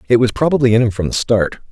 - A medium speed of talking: No, fast, 280 wpm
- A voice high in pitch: No, low, 120 Hz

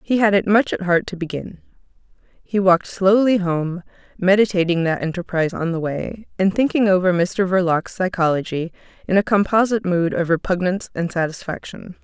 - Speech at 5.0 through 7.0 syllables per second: Yes, 5.4 syllables/s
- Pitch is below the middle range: No, medium, 185 Hz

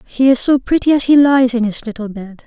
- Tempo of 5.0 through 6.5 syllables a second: Yes, 5.6 syllables/s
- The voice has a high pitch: Yes, very high, 250 Hz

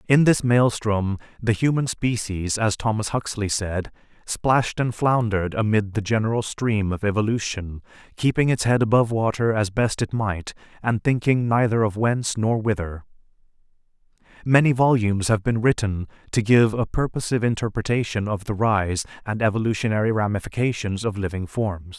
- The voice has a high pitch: No, low, 110 Hz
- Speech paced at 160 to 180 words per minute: No, average, 145 wpm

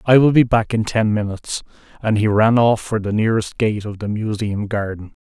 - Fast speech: Yes, fast, 220 wpm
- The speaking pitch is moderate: No, low, 110 Hz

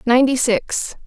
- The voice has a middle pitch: No, very high, 250 Hz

